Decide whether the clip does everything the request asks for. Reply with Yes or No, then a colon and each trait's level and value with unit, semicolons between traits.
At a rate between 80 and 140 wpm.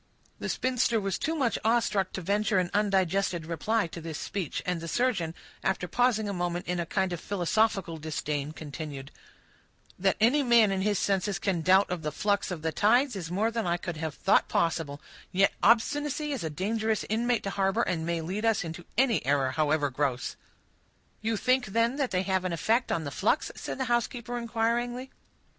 No: average, 190 wpm